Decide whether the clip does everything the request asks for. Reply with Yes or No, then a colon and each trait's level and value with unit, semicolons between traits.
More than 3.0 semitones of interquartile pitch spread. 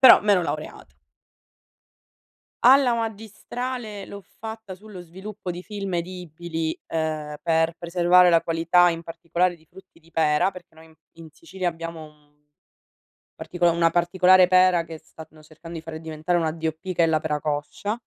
No: narrow, 2.6 semitones